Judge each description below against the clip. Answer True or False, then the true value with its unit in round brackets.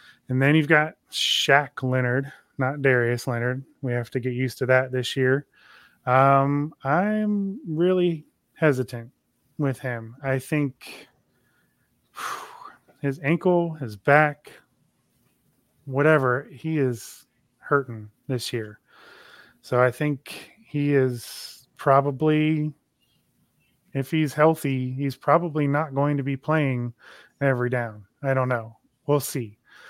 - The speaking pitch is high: False (135 Hz)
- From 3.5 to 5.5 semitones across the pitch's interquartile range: False (3.0 semitones)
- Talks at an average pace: False (120 wpm)